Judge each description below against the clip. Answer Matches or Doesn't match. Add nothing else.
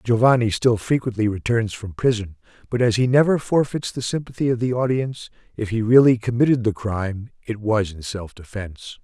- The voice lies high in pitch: Doesn't match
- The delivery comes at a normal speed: Matches